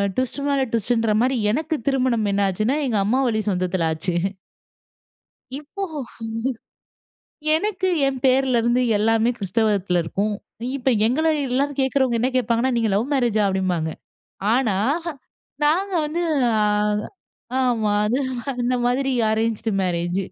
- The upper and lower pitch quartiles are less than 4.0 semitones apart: No, average, 4.3 semitones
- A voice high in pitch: Yes, high, 235 Hz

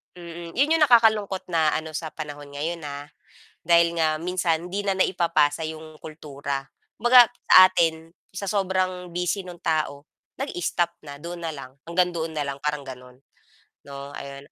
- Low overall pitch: No, medium, 165 Hz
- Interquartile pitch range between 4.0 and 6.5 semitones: No, average, 3.4 semitones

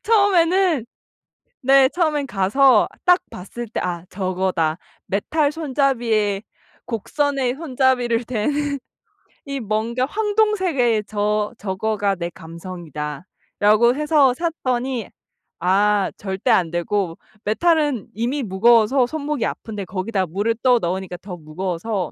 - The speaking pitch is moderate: No, high, 225 Hz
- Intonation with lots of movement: Yes, wide, 6.4 semitones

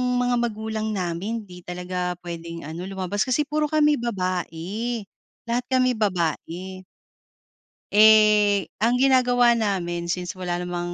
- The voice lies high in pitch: Yes, high, 205 Hz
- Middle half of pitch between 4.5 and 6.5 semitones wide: Yes, average, 5.0 semitones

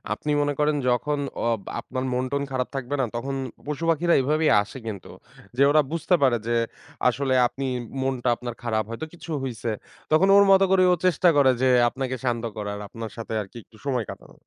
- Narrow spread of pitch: No, average, 4.0 semitones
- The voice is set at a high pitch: No, low, 130 Hz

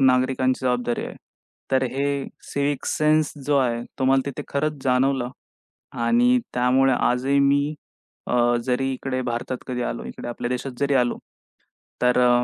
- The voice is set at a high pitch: No, low, 130 Hz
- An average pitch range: No, narrow, 2.1 semitones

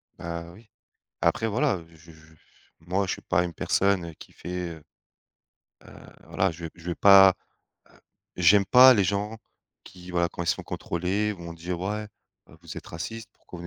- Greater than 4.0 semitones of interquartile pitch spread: No, average, 3.0 semitones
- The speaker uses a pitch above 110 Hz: No, very low, 90 Hz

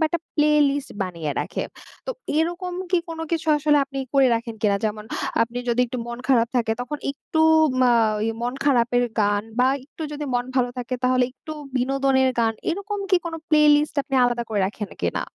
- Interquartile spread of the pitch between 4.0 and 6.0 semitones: Yes, average, 4.3 semitones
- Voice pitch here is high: Yes, very high, 255 Hz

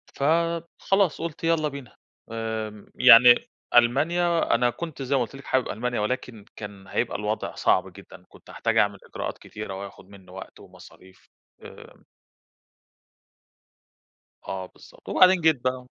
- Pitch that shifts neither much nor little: No, wide, 6.6 semitones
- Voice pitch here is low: Yes, low, 125 Hz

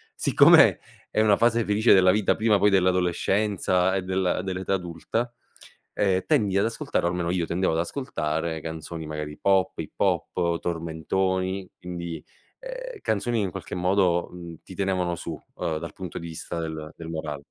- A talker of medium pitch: No, very low, 90 Hz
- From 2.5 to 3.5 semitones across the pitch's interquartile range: Yes, average, 2.8 semitones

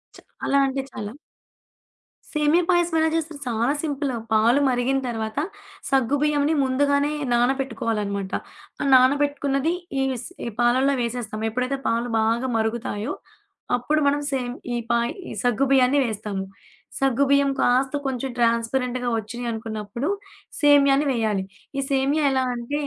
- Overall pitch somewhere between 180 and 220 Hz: No, very high, 255 Hz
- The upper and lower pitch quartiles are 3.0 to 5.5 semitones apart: Yes, average, 3.3 semitones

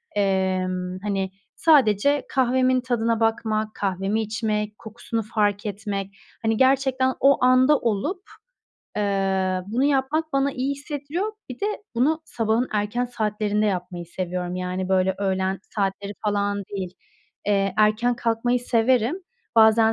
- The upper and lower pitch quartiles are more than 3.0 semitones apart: Yes, average, 4.5 semitones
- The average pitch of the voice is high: Yes, high, 215 Hz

